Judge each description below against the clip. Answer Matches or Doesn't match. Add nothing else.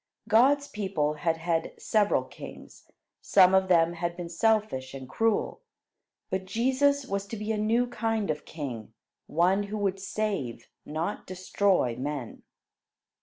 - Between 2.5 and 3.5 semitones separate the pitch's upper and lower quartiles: Doesn't match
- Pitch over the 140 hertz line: Matches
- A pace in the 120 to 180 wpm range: Matches